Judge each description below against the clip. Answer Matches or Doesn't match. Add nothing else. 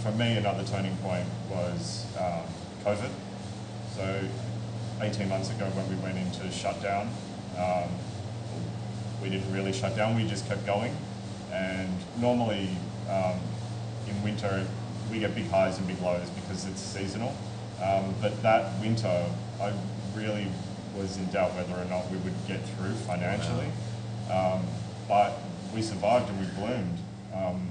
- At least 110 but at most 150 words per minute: Matches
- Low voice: Matches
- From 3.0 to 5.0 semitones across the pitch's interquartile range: Doesn't match